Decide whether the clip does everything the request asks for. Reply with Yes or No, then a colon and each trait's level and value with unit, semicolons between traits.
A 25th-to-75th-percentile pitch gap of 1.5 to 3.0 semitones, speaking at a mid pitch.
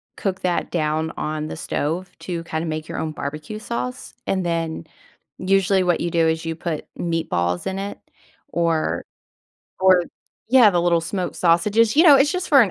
No: average, 3.4 semitones; medium, 170 Hz